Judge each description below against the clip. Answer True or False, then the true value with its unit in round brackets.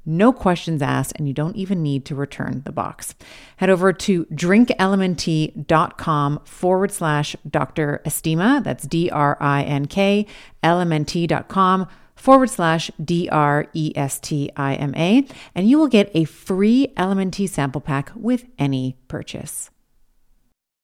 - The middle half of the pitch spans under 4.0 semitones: False (4.8 semitones)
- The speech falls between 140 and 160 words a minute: True (155 wpm)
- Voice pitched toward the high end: False (165 Hz)